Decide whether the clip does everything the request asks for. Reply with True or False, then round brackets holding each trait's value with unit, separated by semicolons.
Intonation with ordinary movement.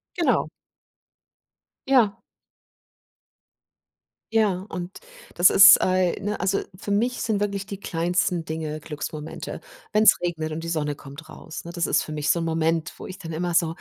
True (3.7 semitones)